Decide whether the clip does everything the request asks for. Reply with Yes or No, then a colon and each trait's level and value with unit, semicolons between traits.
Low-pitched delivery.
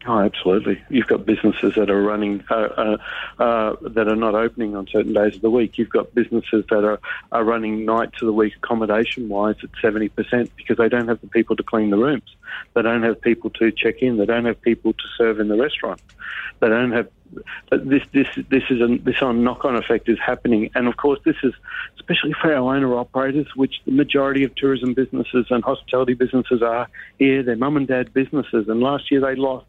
Yes: low, 115 Hz